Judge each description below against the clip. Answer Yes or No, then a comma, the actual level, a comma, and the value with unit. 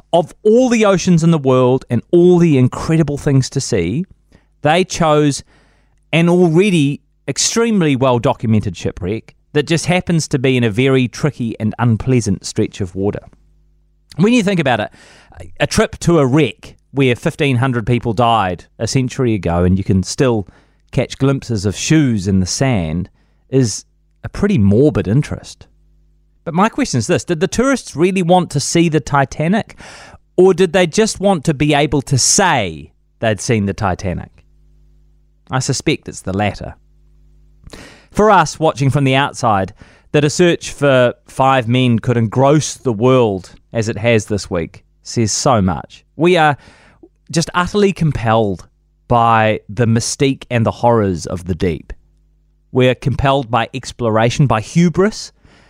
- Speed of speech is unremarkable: Yes, average, 160 wpm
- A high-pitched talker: No, low, 125 Hz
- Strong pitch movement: Yes, wide, 6.8 semitones